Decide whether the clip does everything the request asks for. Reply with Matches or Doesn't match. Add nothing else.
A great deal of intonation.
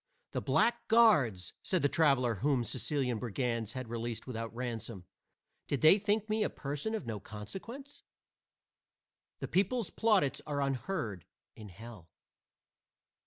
Matches